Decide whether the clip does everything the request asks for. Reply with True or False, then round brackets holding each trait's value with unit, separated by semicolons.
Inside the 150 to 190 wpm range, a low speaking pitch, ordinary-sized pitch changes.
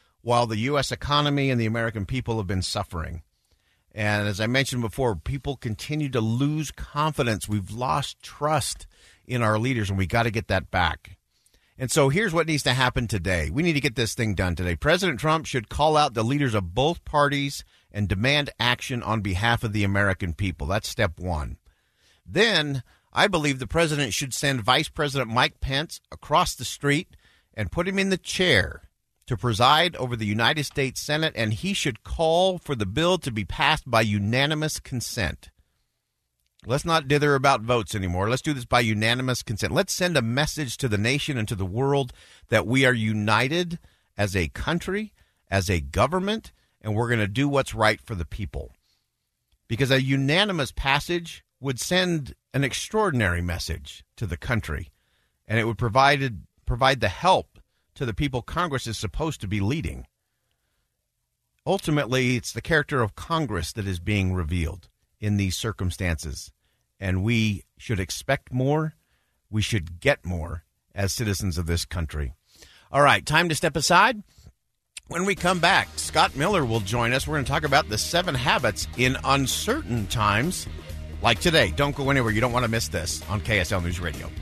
False (180 wpm; 120 Hz; 6.5 semitones)